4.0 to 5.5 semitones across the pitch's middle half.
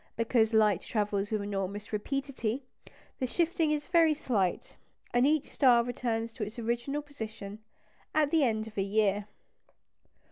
Yes: average, 4.8 semitones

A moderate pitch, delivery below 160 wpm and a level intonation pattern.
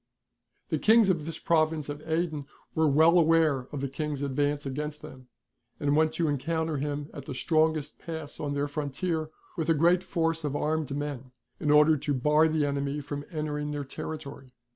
No: medium, 150 Hz; average, 185 wpm; narrow, 1.9 semitones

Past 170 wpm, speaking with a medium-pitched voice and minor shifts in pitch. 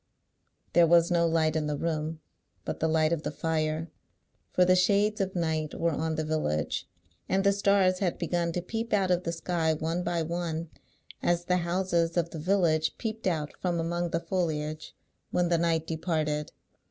Yes: average, 185 wpm; medium, 170 Hz; narrow, 2.2 semitones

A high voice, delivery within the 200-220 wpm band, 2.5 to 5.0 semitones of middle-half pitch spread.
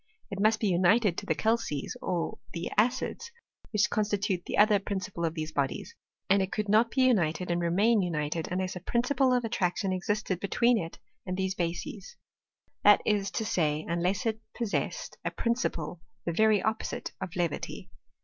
No: high, 195 Hz; average, 175 wpm; average, 4.0 semitones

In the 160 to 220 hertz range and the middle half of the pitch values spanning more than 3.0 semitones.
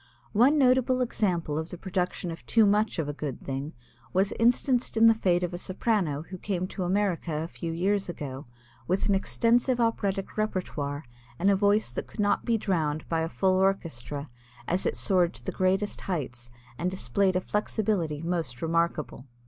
Yes: medium, 185 Hz; average, 4.2 semitones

